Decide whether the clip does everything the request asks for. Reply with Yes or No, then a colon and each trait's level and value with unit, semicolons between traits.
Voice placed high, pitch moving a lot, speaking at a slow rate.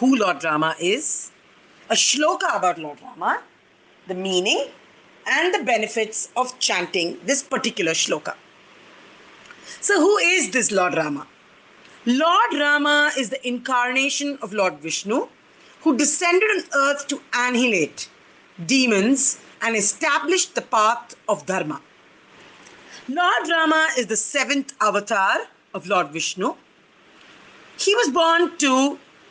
Yes: very high, 255 Hz; wide, 6.4 semitones; slow, 120 wpm